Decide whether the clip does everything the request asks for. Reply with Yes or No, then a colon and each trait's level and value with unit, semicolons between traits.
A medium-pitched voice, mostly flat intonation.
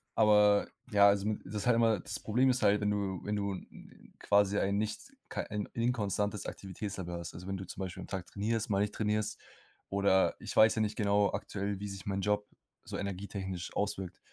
No: low, 100 Hz; narrow, 1.3 semitones